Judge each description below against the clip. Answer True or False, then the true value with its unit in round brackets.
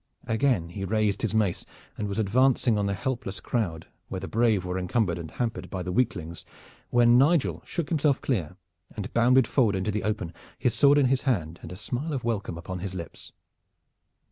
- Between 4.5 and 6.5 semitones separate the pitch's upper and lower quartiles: True (5.1 semitones)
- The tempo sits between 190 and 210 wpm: True (195 wpm)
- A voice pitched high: False (105 Hz)